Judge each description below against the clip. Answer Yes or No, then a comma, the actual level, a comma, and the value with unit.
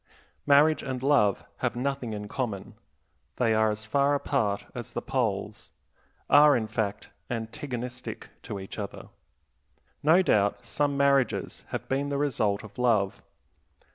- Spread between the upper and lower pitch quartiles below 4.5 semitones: No, average, 4.8 semitones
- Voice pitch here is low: Yes, low, 125 Hz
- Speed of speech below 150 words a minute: Yes, average, 140 wpm